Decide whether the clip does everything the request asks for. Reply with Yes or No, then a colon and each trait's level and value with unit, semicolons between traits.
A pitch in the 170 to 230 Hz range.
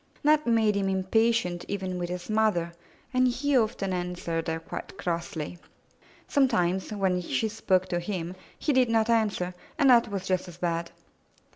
Yes: high, 190 Hz